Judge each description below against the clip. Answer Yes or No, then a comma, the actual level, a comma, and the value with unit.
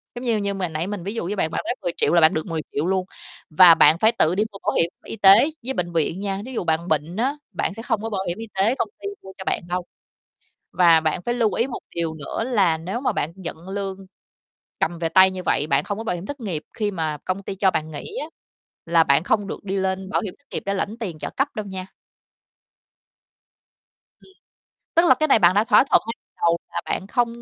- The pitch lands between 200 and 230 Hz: No, high, 190 Hz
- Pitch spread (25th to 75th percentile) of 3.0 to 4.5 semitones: Yes, average, 4.1 semitones